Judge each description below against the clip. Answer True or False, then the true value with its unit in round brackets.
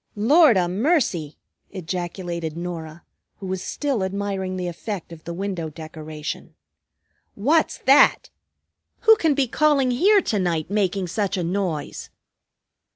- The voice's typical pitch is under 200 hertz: True (190 Hz)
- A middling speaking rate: False (130 wpm)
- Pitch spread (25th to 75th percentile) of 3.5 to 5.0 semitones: False (5.5 semitones)